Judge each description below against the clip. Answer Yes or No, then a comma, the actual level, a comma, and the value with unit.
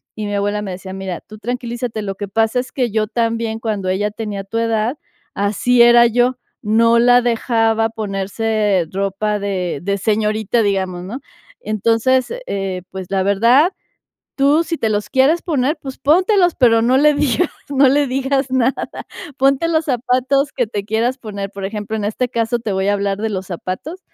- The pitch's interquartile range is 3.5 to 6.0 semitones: Yes, average, 4.0 semitones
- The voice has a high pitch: Yes, high, 225 Hz